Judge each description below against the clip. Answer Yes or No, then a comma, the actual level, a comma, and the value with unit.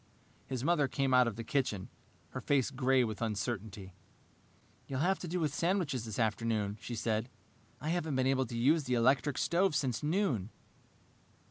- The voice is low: Yes, low, 130 Hz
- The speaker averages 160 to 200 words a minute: Yes, average, 170 wpm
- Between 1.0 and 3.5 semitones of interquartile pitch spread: No, average, 4.5 semitones